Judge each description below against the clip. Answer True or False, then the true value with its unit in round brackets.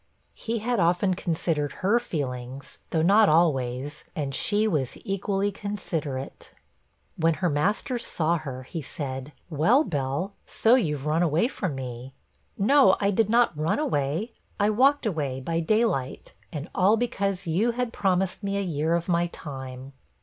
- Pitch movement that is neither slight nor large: False (6.1 semitones)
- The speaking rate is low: False (155 wpm)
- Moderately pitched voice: True (170 Hz)